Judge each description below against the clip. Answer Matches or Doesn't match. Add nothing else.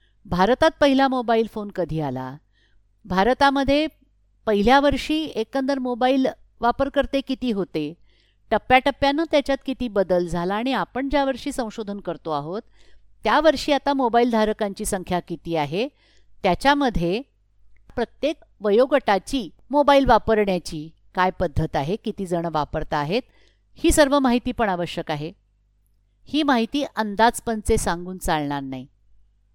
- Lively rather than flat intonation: Matches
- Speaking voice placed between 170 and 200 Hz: Doesn't match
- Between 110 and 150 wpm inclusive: Matches